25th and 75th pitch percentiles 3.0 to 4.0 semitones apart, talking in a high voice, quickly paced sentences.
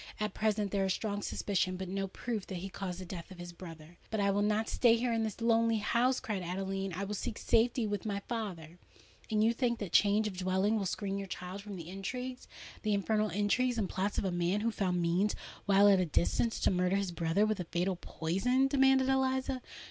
Yes: average, 3.3 semitones; high, 200 Hz; fast, 215 wpm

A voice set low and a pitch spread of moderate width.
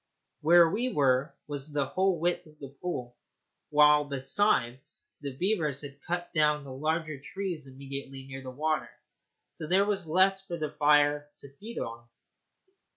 No: medium, 150 Hz; average, 4.0 semitones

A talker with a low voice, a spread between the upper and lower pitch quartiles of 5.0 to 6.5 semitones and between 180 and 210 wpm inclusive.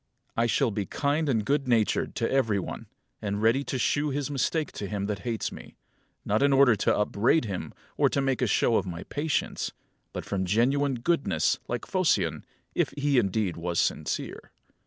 Yes: low, 120 Hz; wide, 5.4 semitones; average, 185 wpm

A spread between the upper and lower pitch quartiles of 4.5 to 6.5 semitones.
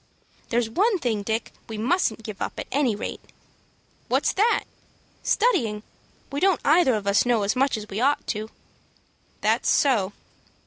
Yes: wide, 5.4 semitones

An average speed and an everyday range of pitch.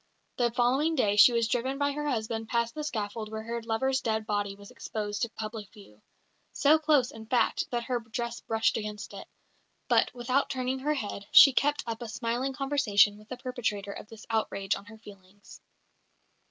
Yes: average, 190 wpm; average, 3.5 semitones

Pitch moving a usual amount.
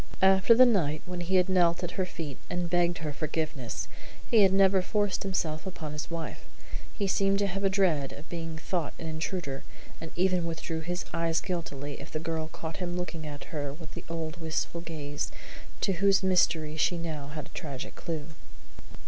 Yes: average, 3.1 semitones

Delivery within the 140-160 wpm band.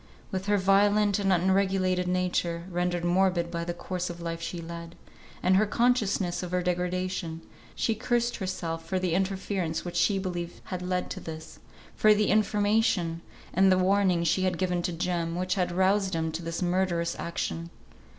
No: average, 175 wpm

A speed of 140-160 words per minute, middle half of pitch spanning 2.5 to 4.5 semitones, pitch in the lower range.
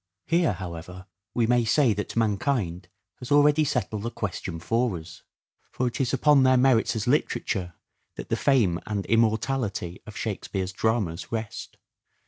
No: average, 150 wpm; average, 5.2 semitones; low, 110 Hz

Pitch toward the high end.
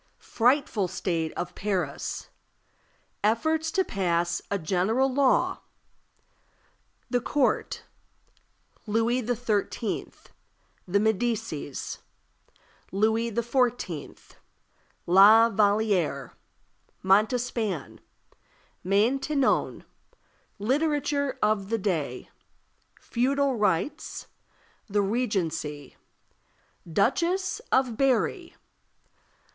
Yes: high, 220 Hz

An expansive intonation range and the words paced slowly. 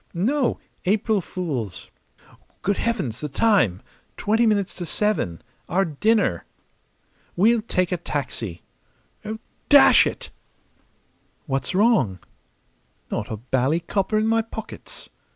Yes: wide, 8.6 semitones; slow, 110 wpm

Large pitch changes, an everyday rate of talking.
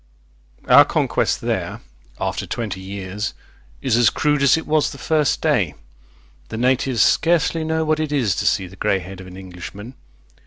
Yes: wide, 7.8 semitones; average, 170 wpm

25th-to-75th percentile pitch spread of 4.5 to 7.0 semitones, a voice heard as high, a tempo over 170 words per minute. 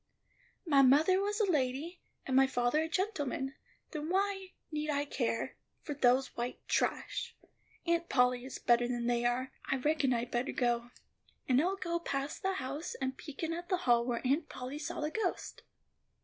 Yes: average, 5.2 semitones; very high, 280 Hz; average, 180 wpm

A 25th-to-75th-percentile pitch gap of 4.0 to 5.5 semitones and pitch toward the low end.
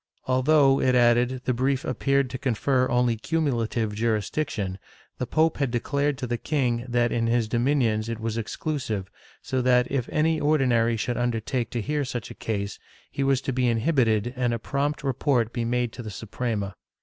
No: average, 2.9 semitones; low, 125 Hz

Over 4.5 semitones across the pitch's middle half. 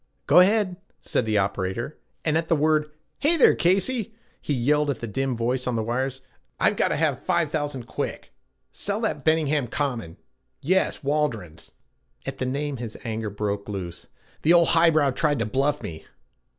Yes: wide, 5.5 semitones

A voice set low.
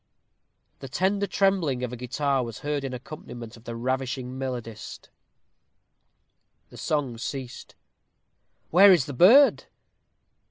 Yes: low, 130 Hz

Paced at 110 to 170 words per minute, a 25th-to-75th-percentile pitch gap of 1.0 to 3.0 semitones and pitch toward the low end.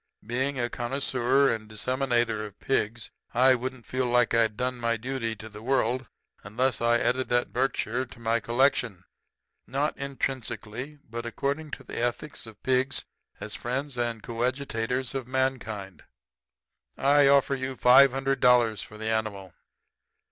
Yes: average, 150 wpm; narrow, 2.6 semitones; low, 125 Hz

